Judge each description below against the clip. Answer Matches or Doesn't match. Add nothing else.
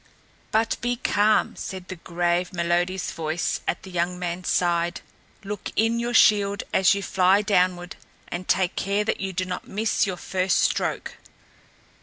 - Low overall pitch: Doesn't match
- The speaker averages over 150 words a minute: Matches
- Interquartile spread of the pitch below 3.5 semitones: Matches